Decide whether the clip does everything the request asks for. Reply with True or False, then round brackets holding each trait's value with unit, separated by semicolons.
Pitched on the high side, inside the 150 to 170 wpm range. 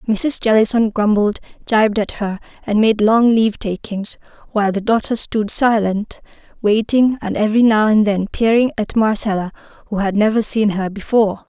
True (215 Hz; 160 wpm)